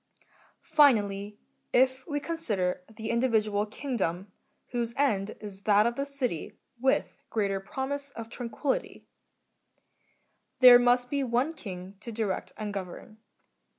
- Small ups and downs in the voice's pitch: No, average, 4.4 semitones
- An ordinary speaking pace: No, slow, 130 wpm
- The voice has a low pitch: No, high, 230 Hz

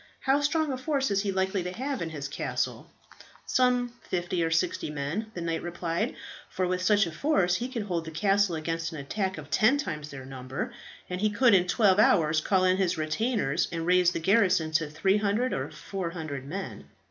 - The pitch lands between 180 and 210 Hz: Yes, medium, 185 Hz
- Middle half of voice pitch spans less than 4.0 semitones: No, average, 4.4 semitones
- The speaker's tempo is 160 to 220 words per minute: Yes, average, 200 wpm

